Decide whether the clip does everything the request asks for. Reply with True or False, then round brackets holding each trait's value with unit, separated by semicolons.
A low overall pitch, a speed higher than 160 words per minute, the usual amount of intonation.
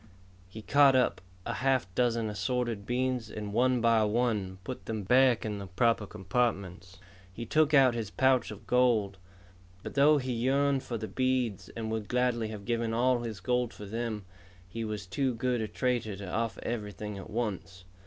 True (115 Hz; 180 wpm; 3.2 semitones)